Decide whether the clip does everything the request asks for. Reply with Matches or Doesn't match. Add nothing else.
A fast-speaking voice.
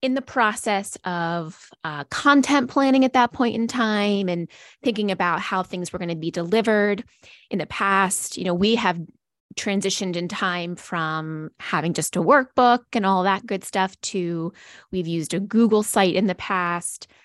Doesn't match